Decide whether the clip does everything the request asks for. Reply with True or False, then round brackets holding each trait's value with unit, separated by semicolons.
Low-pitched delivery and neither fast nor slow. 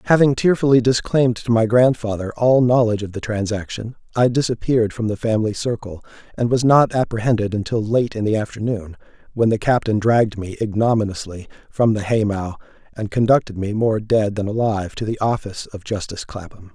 True (110 Hz; 170 wpm)